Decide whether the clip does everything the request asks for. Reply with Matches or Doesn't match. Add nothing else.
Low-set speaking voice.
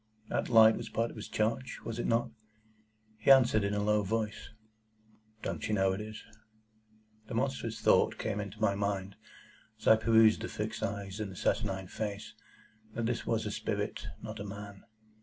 Matches